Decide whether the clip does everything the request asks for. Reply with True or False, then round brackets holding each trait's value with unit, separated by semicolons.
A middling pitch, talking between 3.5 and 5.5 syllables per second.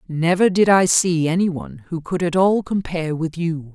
True (170 Hz; 4.7 syllables/s)